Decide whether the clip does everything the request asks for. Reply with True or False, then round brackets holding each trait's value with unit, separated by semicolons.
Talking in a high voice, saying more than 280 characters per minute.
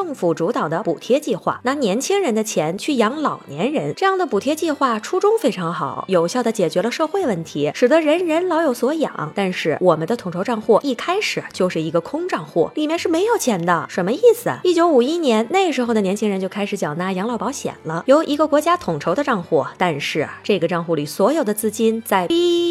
True (235 Hz; 335 characters per minute)